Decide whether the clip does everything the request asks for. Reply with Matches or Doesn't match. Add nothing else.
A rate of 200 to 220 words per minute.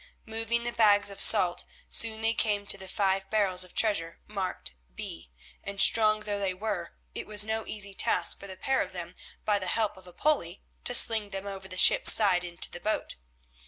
Matches